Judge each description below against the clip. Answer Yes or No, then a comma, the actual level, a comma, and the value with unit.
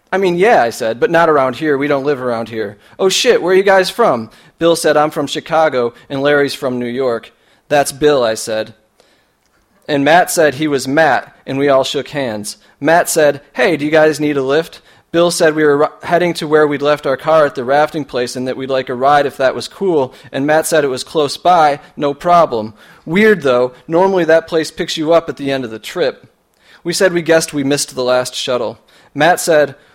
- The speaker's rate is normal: No, fast, 230 wpm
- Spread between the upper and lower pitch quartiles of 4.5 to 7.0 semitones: No, average, 3.5 semitones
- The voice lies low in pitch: No, medium, 150 Hz